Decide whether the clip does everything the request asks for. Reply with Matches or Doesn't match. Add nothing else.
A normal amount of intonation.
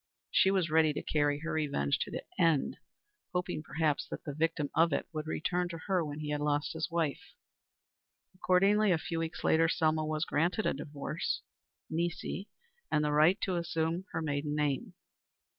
Doesn't match